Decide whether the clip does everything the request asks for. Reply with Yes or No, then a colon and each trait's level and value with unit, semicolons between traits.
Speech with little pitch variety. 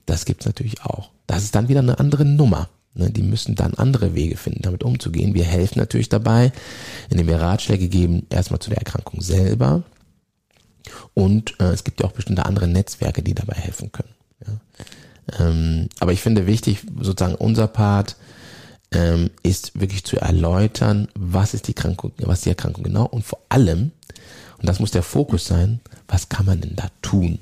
No: average, 4.2 semitones